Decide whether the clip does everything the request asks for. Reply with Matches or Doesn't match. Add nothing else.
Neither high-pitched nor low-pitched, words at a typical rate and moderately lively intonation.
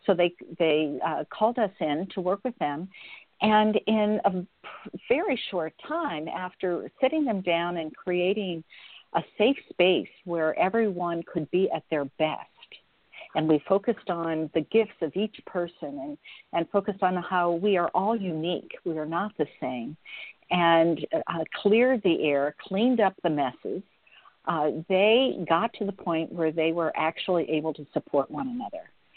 Matches